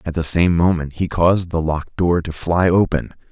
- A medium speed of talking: No, fast, 215 wpm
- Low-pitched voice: Yes, very low, 85 Hz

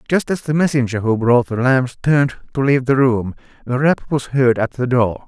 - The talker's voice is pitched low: Yes, low, 130 Hz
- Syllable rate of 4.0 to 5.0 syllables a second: No, 5.3 syllables/s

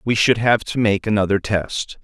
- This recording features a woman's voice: No, male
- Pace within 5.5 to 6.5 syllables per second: No, 4.7 syllables/s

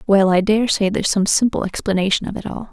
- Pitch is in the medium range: No, high, 200 Hz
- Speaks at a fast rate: Yes, fast, 220 wpm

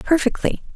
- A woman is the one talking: Yes, female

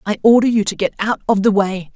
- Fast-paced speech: Yes, fast, 275 wpm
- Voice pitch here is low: No, high, 210 Hz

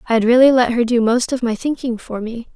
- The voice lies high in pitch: Yes, high, 240 Hz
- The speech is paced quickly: Yes, fast, 280 wpm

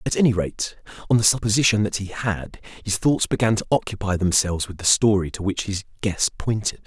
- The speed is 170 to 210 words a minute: Yes, average, 200 wpm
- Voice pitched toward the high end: No, low, 100 Hz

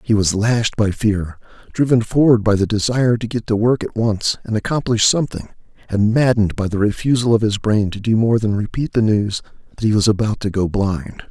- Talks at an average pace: No, fast, 220 wpm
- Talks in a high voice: No, low, 110 Hz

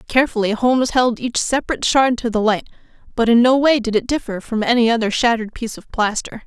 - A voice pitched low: No, high, 235 Hz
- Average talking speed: No, fast, 215 wpm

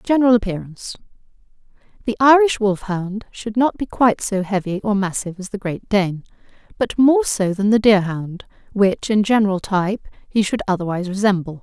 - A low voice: No, high, 205 Hz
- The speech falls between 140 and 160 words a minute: Yes, average, 155 wpm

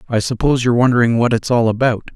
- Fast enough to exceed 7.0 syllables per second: Yes, 7.5 syllables/s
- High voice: No, low, 115 Hz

